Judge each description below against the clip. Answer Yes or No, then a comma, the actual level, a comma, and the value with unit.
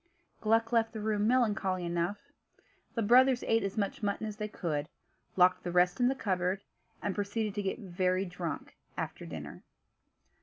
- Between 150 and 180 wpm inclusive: Yes, average, 165 wpm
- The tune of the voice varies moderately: Yes, average, 3.5 semitones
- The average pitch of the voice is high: Yes, high, 205 Hz